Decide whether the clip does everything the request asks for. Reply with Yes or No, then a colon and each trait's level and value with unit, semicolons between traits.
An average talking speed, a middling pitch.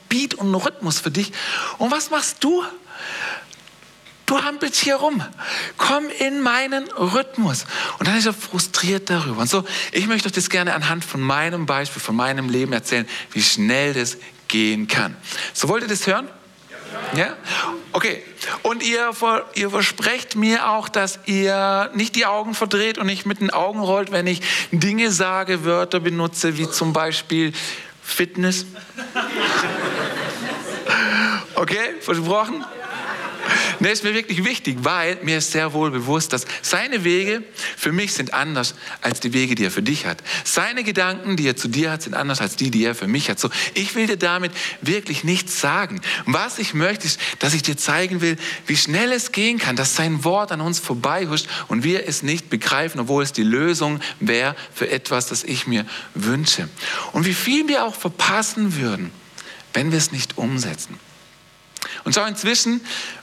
Yes: average, 175 wpm; medium, 180 Hz